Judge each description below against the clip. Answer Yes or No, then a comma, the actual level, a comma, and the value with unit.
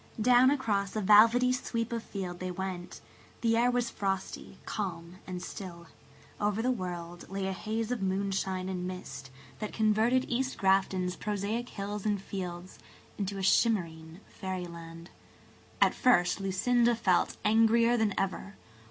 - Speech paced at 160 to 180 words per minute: No, average, 150 wpm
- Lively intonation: No, average, 3.7 semitones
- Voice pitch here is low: No, high, 195 Hz